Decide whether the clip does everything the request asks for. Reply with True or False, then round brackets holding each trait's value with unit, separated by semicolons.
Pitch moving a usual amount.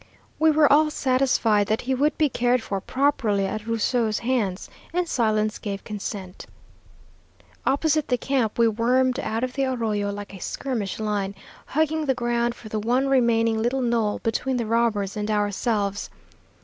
True (3.8 semitones)